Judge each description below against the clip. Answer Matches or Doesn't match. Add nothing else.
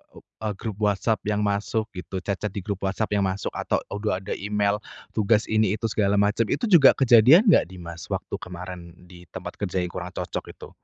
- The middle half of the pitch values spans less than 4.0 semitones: Matches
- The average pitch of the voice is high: Doesn't match